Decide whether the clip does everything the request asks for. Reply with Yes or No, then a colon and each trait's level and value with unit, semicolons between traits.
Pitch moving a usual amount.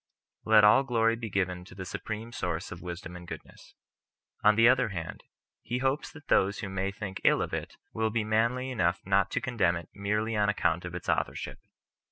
Yes: average, 4.0 semitones